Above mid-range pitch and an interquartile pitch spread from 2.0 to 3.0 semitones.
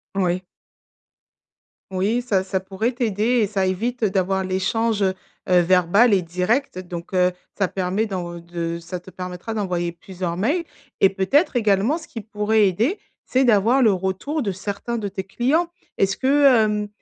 No: high, 195 Hz; average, 3.6 semitones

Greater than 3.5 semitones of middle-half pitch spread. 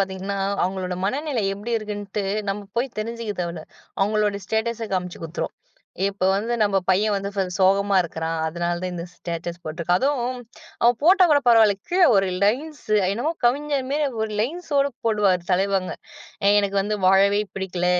Yes: average, 3.9 semitones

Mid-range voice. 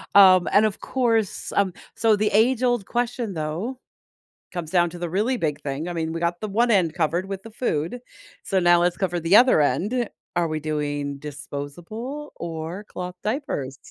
Yes: medium, 180 Hz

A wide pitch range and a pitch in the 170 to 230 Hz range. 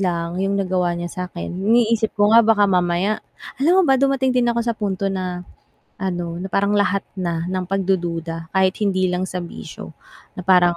No: average, 2.8 semitones; medium, 185 Hz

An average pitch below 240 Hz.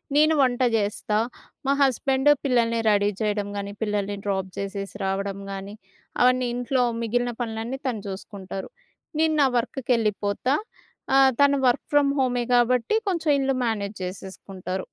Yes: high, 230 Hz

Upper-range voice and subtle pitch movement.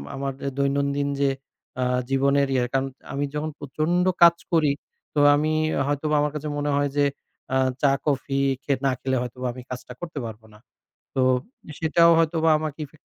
No: medium, 140 Hz; narrow, 2.2 semitones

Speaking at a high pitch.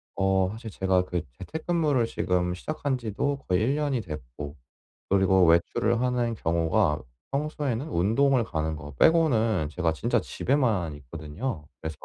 No: very low, 95 Hz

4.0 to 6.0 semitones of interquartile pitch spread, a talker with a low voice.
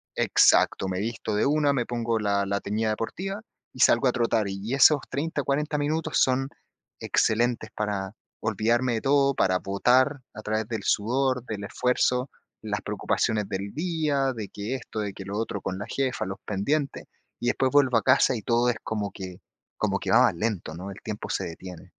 Yes: average, 4.7 semitones; low, 115 Hz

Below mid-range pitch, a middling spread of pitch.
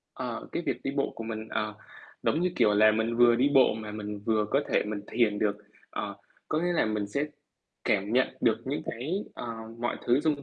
Yes: low, 115 Hz; average, 4.1 semitones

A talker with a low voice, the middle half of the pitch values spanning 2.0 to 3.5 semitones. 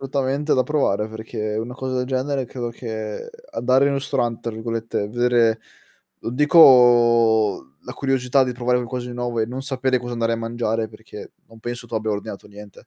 Yes: low, 120 Hz; narrow, 2.5 semitones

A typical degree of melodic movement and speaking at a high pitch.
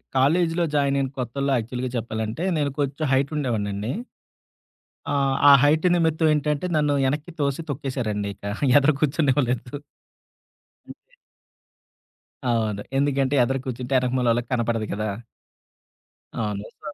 No: average, 3.8 semitones; low, 135 Hz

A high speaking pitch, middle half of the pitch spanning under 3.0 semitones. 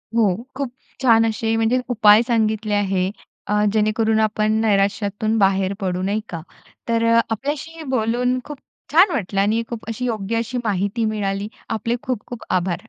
Yes: high, 220 Hz; narrow, 2.4 semitones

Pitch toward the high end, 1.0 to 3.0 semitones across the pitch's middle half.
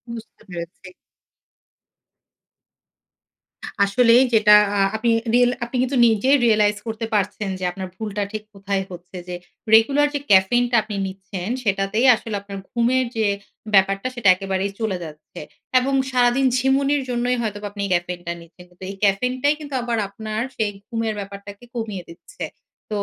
No: high, 210 Hz; average, 3.7 semitones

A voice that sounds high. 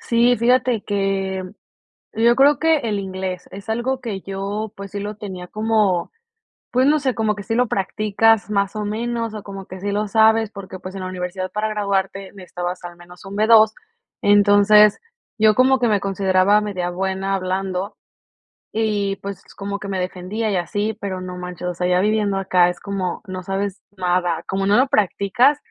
Yes: high, 200 Hz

